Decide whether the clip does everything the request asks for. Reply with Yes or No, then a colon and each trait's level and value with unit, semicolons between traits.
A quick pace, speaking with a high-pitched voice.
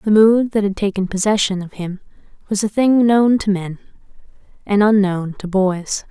No: average, 175 wpm; high, 200 Hz